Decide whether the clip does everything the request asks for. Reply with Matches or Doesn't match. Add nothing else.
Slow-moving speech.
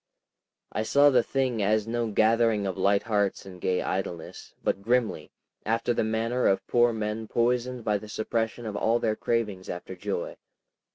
Doesn't match